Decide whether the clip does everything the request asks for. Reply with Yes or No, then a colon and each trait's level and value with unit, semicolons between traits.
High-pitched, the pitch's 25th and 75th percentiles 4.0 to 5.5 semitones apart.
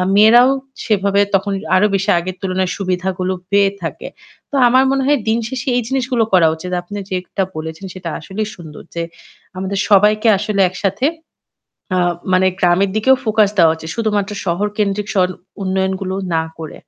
No: high, 195 Hz; narrow, 2.6 semitones